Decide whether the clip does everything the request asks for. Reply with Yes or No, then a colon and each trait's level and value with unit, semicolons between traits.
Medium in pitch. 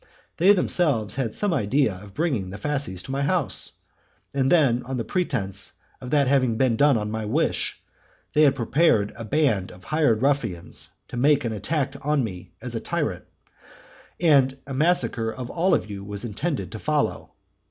No: low, 130 Hz